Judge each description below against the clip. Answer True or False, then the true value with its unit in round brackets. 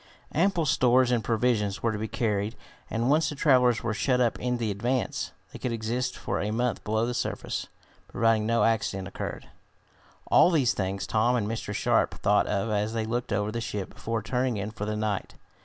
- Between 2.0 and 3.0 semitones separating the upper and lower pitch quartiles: True (2.7 semitones)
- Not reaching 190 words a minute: False (200 wpm)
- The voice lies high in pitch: False (115 Hz)